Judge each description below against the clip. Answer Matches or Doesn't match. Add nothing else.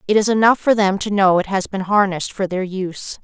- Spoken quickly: Matches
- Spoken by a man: Doesn't match